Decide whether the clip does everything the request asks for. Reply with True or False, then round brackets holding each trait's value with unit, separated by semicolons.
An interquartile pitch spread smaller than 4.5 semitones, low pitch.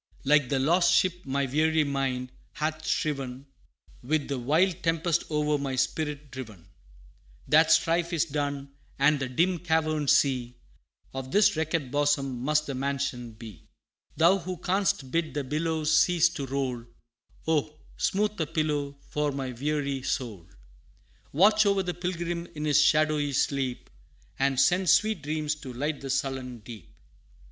False (3.3 semitones; 145 Hz)